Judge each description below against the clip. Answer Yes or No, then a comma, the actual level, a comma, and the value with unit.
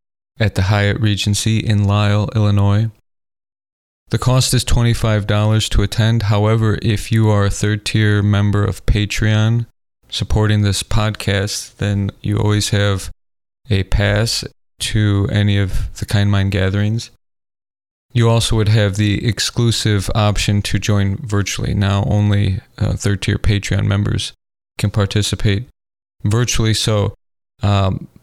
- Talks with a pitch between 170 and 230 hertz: No, low, 105 Hz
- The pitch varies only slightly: Yes, narrow, 1.5 semitones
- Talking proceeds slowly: Yes, slow, 130 wpm